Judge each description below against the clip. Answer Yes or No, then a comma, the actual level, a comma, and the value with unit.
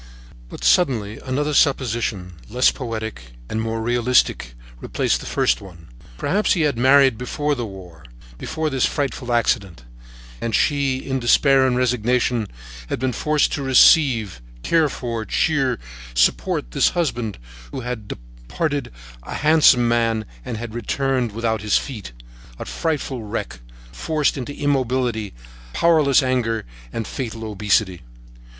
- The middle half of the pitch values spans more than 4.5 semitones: No, average, 4.0 semitones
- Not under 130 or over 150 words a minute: Yes, slow, 135 wpm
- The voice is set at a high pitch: No, low, 120 Hz